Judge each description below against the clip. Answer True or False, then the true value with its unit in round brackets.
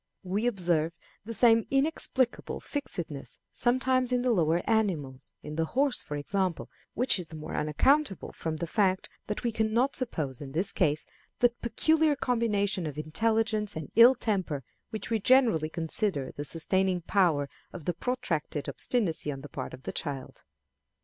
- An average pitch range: False (7.2 semitones)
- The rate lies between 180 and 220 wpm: False (165 wpm)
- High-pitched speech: True (195 Hz)